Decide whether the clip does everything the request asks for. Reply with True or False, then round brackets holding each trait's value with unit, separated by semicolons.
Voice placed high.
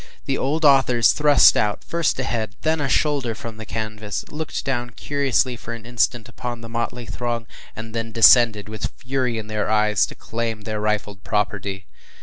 False (115 Hz)